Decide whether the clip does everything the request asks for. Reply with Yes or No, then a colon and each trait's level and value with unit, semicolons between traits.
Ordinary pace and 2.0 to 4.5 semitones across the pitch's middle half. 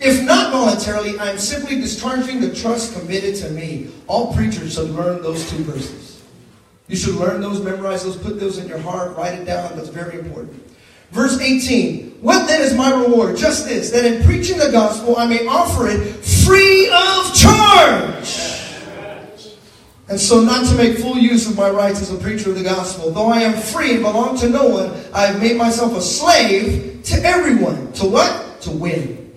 No: average, 190 wpm; average, 5.2 semitones